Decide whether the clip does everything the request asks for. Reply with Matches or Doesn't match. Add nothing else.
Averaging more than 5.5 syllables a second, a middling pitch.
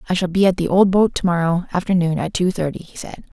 Matches